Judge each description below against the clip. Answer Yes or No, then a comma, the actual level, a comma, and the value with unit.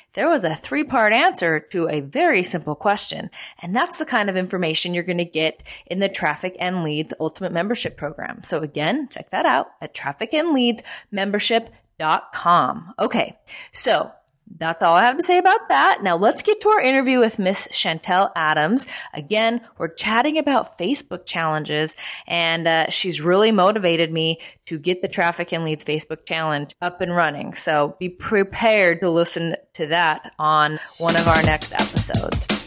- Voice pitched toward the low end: No, medium, 180 Hz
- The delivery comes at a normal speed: Yes, average, 170 wpm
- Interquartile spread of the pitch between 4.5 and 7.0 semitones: Yes, wide, 5.5 semitones